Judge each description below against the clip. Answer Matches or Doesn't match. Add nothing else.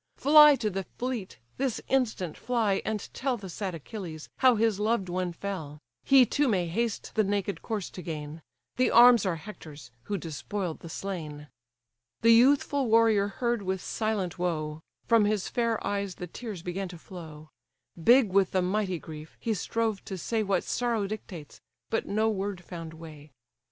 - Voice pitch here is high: Matches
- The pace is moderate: Matches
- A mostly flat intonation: Doesn't match